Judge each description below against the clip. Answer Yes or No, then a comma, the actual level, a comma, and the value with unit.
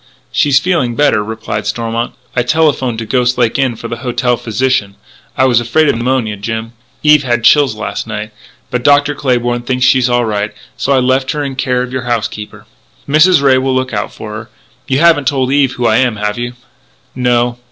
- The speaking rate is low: No, average, 200 wpm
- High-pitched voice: No, low, 125 Hz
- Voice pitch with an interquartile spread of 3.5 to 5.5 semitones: No, narrow, 2.4 semitones